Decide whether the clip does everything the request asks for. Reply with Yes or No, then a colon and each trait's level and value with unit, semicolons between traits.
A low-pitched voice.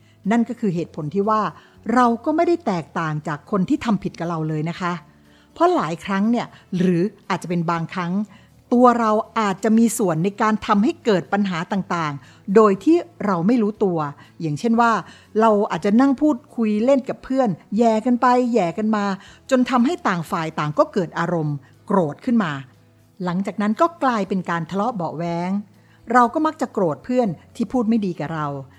No: high, 205 Hz